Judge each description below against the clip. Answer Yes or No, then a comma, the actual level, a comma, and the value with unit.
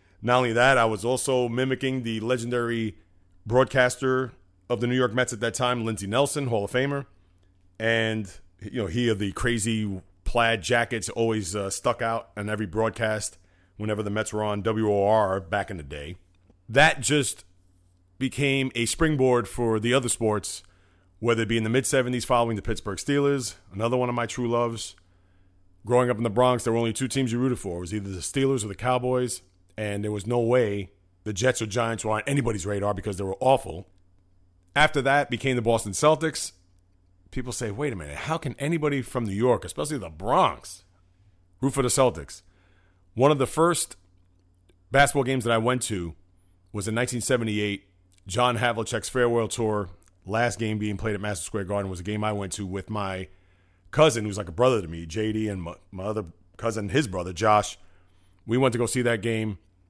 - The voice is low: Yes, low, 110 Hz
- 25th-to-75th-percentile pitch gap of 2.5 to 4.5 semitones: No, average, 4.9 semitones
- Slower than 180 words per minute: No, average, 195 wpm